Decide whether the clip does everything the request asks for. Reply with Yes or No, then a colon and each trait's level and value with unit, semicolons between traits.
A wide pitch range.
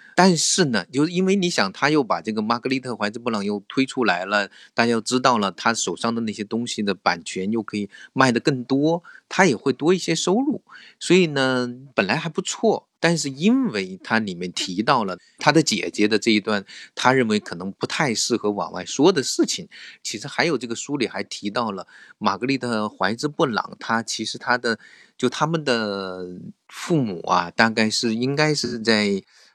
Yes: wide, 6.5 semitones